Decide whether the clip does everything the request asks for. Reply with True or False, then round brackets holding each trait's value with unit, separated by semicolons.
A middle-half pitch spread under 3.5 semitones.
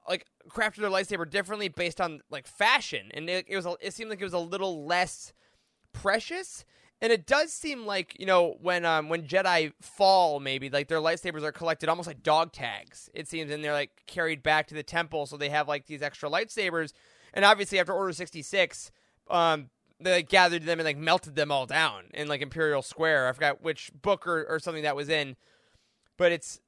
False (4.0 semitones)